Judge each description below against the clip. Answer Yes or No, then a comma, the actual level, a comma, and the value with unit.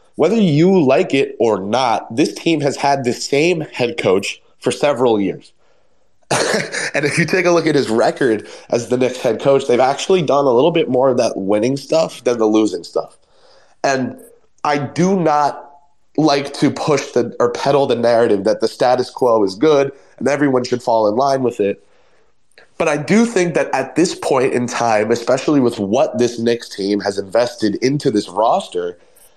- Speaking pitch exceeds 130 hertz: Yes, medium, 140 Hz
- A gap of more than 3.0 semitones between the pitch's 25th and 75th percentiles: Yes, average, 4.9 semitones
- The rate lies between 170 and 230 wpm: Yes, average, 190 wpm